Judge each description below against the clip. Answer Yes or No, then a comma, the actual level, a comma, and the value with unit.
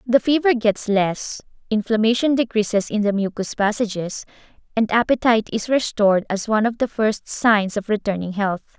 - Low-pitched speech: No, high, 220 Hz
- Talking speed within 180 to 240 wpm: No, average, 155 wpm